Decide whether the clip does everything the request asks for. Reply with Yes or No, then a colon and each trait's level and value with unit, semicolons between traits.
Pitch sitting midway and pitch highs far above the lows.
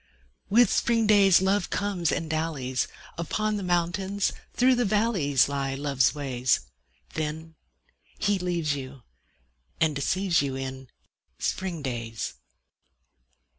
Yes: medium, 165 Hz; wide, 6.3 semitones